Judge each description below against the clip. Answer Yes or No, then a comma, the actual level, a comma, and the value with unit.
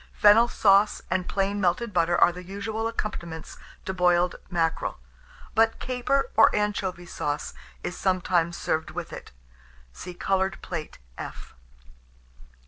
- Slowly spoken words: Yes, slow, 130 wpm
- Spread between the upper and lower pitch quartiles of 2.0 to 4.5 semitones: Yes, average, 3.2 semitones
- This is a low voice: No, medium, 185 Hz